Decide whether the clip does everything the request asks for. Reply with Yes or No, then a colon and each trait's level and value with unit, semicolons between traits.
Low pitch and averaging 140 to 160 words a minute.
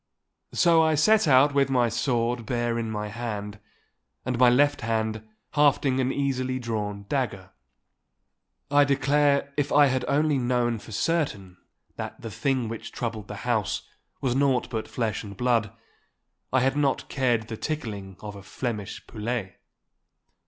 Yes: low, 120 Hz; average, 150 wpm